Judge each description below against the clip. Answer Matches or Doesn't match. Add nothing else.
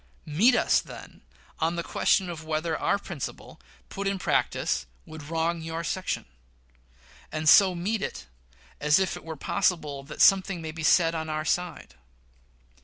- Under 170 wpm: Matches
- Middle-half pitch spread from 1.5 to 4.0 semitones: Matches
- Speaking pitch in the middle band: Matches